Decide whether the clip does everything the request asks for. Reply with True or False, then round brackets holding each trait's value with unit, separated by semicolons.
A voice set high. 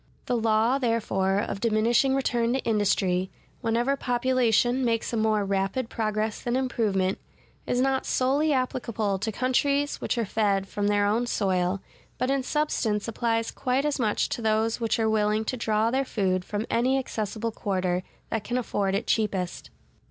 True (225 Hz)